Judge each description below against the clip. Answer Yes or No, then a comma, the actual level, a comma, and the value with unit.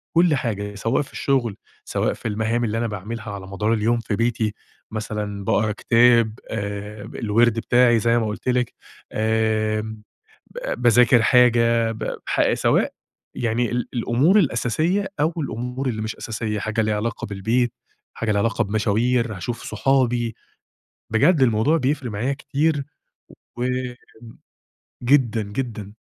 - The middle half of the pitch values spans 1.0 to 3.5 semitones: Yes, narrow, 2.4 semitones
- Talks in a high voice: No, low, 115 Hz